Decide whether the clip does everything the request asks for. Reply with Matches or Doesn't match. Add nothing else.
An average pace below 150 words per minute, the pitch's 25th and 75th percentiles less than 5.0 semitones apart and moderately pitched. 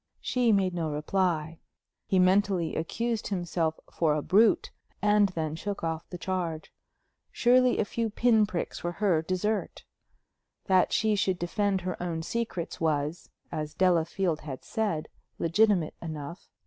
Matches